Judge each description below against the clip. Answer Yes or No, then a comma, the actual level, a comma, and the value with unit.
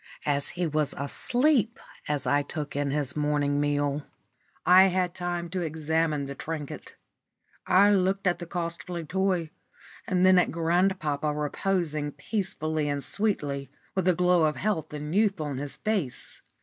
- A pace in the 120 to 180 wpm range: Yes, average, 150 wpm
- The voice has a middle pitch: Yes, medium, 160 Hz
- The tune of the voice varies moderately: Yes, average, 4.0 semitones